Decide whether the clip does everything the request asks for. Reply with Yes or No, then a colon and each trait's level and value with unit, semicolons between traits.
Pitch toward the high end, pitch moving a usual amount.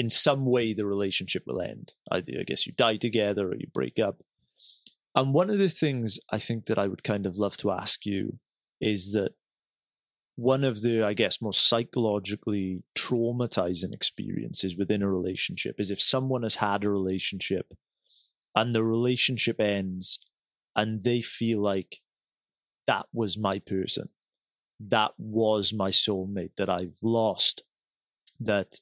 No: low, 110 Hz; average, 3.0 semitones